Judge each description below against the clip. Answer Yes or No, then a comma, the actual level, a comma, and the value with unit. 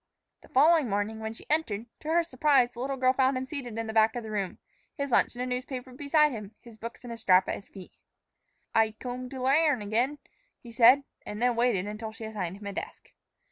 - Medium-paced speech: No, fast, 230 wpm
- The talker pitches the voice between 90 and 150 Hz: No, high, 240 Hz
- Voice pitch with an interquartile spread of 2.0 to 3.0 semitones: No, average, 3.5 semitones